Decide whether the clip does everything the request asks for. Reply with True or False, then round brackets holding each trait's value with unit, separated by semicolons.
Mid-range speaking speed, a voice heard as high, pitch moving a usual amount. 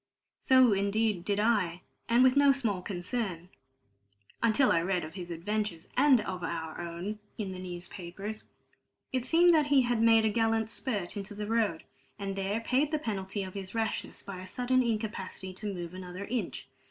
True (175 wpm; 205 Hz; 4.0 semitones)